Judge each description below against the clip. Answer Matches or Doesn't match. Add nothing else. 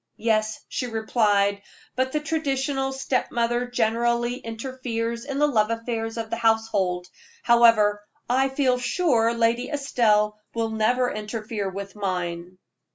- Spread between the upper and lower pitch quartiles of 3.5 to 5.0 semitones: Doesn't match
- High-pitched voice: Matches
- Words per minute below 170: Matches